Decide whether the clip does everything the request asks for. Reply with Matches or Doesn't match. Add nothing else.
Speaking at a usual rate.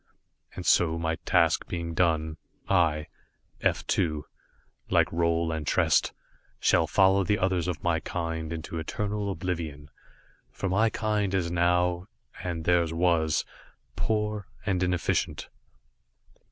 Doesn't match